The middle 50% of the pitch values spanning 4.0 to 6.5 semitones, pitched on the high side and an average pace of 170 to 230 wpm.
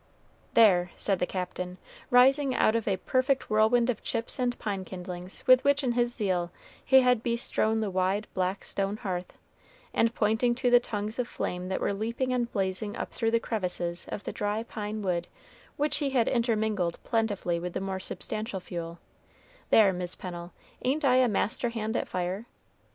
Yes: average, 4.4 semitones; high, 215 Hz; average, 185 wpm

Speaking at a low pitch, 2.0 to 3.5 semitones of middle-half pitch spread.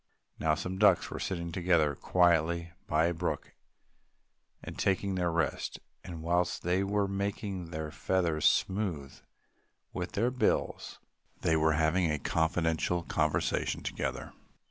Yes: very low, 85 Hz; average, 2.8 semitones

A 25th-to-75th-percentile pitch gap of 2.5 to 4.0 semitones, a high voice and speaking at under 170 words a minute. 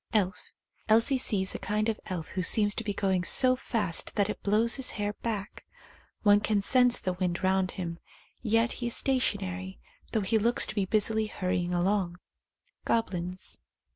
No: average, 3.3 semitones; high, 205 Hz; average, 175 wpm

